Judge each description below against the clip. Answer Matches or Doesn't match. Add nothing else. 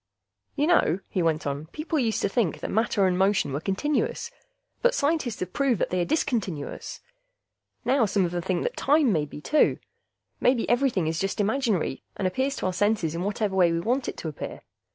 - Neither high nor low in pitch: Doesn't match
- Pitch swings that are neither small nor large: Doesn't match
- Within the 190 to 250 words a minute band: Matches